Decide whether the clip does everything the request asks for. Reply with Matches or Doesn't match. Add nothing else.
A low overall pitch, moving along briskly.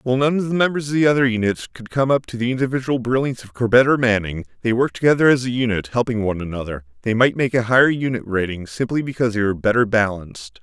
Matches